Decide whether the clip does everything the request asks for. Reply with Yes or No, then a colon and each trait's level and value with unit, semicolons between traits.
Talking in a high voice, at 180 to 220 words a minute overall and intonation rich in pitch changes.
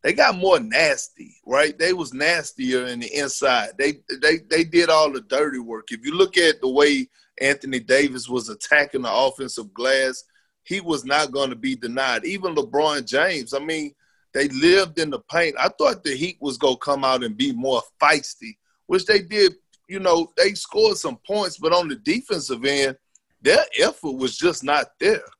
No: medium, 150 Hz; average, 195 wpm; wide, 6.4 semitones